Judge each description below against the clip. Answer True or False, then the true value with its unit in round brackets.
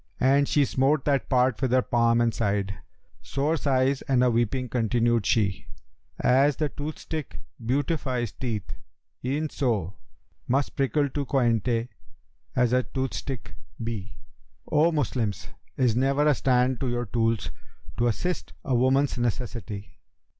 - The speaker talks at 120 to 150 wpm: True (145 wpm)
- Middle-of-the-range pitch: False (125 Hz)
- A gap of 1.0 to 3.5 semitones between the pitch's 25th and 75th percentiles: True (2.9 semitones)